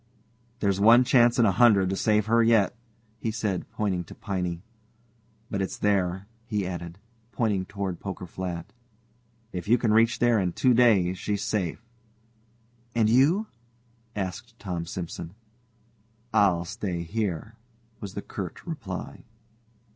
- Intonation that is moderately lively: Yes, average, 3.8 semitones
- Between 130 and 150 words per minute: Yes, average, 140 wpm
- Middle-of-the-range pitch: No, low, 100 Hz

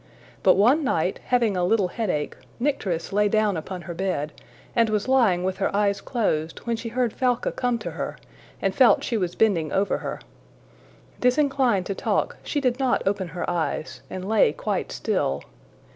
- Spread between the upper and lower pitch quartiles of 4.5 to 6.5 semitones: Yes, average, 5.1 semitones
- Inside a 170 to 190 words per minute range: Yes, average, 175 wpm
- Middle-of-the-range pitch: No, high, 210 Hz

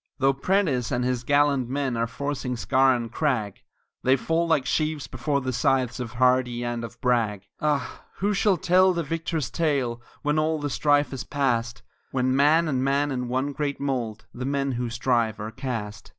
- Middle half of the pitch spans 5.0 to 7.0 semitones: No, average, 3.3 semitones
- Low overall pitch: Yes, low, 130 Hz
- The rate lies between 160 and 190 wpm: Yes, average, 185 wpm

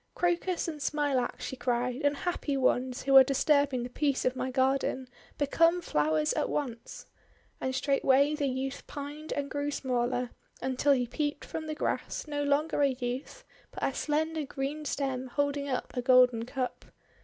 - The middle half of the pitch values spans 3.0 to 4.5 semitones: No, narrow, 2.4 semitones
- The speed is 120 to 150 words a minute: No, average, 165 wpm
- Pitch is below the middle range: No, very high, 275 Hz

